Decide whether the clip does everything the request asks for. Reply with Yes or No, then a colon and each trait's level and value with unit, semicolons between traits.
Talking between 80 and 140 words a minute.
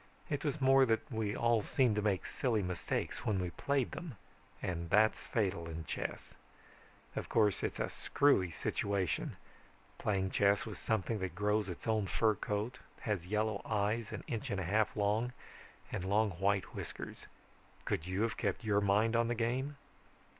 No: average, 170 wpm